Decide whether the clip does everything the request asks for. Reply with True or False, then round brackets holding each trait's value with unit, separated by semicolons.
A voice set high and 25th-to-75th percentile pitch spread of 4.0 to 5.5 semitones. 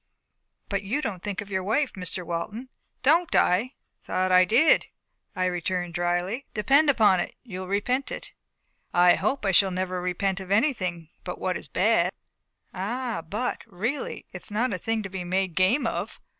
True (195 Hz; 4.5 semitones)